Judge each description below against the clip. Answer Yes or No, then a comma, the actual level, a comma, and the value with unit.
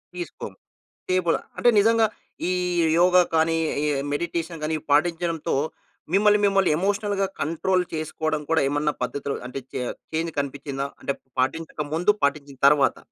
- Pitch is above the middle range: No, medium, 165 Hz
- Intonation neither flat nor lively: Yes, average, 4.0 semitones